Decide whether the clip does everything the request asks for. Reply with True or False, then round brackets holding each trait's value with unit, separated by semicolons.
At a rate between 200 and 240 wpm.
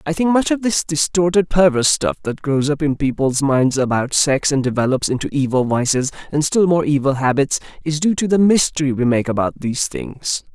True (205 wpm)